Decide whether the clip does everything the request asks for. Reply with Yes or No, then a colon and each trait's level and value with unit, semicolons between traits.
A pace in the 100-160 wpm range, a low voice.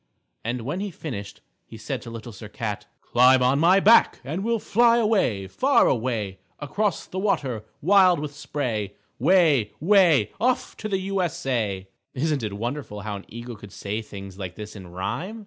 No: average, 185 wpm; low, 130 Hz